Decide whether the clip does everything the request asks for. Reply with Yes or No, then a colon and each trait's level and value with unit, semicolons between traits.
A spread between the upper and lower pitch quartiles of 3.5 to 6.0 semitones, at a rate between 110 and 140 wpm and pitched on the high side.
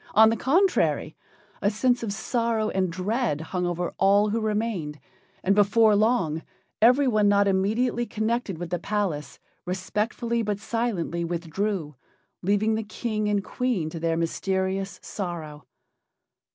Yes: average, 4.1 semitones; slow, 135 wpm; high, 205 Hz